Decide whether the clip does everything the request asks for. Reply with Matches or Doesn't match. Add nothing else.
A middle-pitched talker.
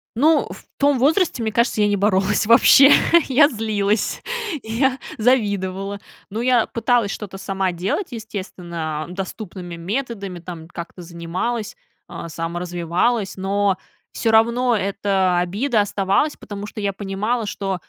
Doesn't match